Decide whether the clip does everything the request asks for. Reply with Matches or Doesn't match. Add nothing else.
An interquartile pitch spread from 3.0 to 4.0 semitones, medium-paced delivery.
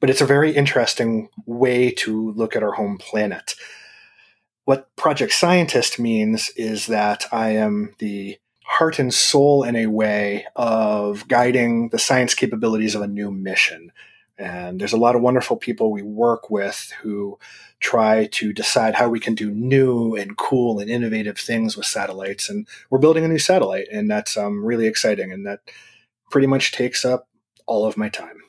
Matches